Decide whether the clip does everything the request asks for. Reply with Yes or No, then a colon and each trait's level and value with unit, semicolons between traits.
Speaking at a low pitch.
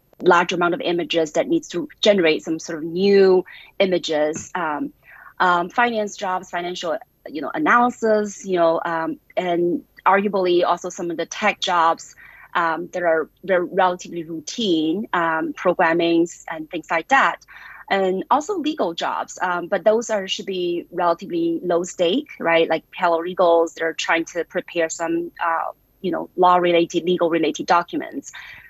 No: medium, 175 Hz